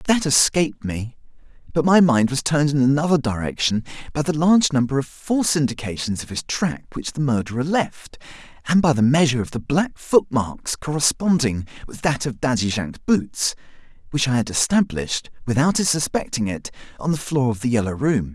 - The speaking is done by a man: Yes, male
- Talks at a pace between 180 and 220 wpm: Yes, average, 185 wpm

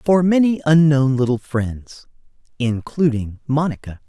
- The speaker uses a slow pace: Yes, slow, 105 wpm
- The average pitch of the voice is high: No, medium, 140 Hz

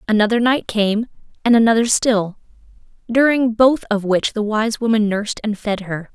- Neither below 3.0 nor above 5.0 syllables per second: Yes, 4.9 syllables/s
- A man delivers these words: No, female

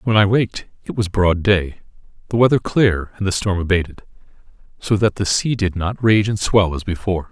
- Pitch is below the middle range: Yes, low, 100 Hz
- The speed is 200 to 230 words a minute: Yes, fast, 205 wpm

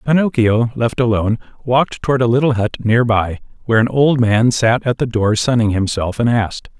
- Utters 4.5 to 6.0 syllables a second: Yes, 5.5 syllables/s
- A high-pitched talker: No, low, 120 Hz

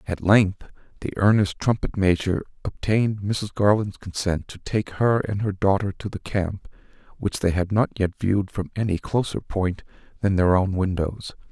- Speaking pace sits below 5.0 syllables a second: Yes, 4.7 syllables/s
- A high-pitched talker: No, low, 100 Hz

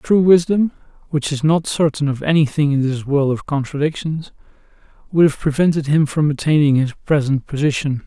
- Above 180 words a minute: No, average, 165 wpm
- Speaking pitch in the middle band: Yes, medium, 150 Hz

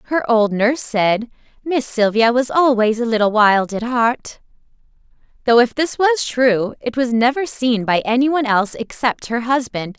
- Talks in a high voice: Yes, high, 240 Hz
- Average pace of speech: Yes, average, 170 wpm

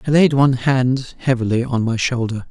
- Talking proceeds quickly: No, average, 190 wpm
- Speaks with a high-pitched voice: No, low, 125 Hz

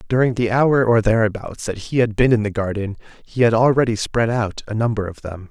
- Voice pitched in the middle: No, low, 110 Hz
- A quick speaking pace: Yes, fast, 230 wpm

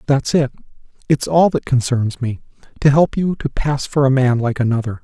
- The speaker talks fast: No, average, 190 wpm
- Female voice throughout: No, male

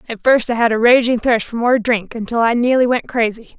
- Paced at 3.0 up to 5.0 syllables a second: No, 5.6 syllables/s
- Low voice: No, high, 235 Hz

